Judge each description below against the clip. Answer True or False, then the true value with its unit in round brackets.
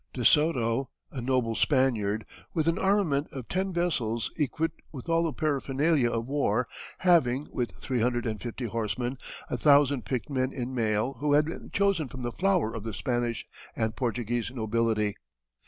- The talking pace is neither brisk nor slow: True (170 wpm)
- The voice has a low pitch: True (130 Hz)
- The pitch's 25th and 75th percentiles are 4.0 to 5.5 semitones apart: True (4.3 semitones)